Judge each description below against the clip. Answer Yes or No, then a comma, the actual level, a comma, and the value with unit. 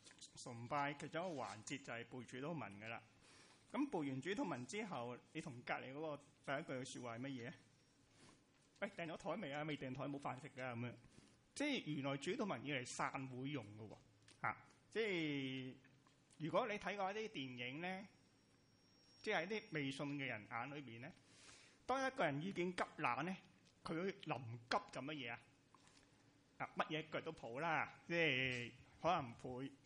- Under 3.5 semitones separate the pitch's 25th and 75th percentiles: No, average, 4.1 semitones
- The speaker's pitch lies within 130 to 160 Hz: Yes, medium, 140 Hz